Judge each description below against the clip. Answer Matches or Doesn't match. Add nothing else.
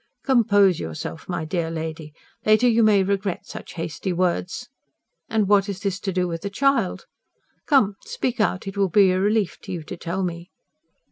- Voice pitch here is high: Matches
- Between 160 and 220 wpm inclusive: Matches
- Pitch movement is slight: Doesn't match